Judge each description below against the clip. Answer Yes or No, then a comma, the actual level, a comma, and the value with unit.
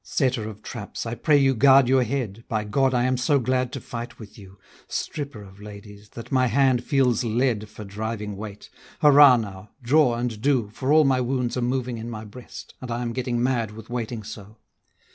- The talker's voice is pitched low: Yes, low, 120 Hz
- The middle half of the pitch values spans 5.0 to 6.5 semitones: No, average, 3.2 semitones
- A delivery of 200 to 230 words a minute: Yes, fast, 205 wpm